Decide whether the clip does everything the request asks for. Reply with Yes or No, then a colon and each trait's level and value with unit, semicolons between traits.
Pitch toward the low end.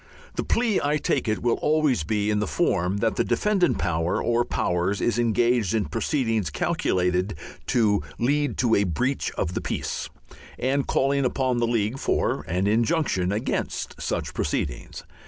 Yes: low, 115 Hz